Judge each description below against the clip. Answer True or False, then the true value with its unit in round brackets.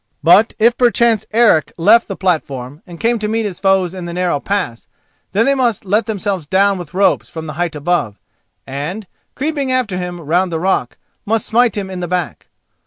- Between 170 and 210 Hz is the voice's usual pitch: True (190 Hz)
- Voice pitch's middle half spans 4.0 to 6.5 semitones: True (4.3 semitones)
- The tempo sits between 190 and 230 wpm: True (195 wpm)